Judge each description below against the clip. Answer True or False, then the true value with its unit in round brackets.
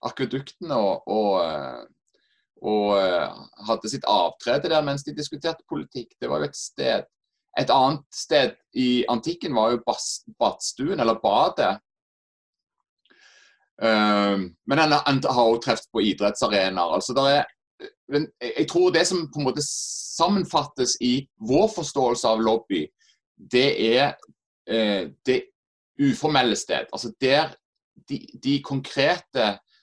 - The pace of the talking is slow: True (120 wpm)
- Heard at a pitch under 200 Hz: True (135 Hz)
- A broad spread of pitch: True (5.7 semitones)